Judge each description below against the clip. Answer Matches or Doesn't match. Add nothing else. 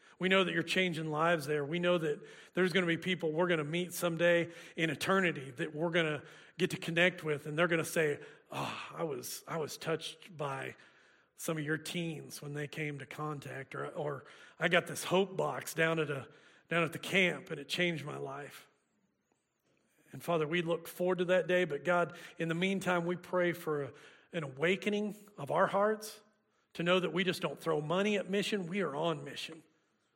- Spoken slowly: Doesn't match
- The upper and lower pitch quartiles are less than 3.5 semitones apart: Matches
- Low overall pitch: Doesn't match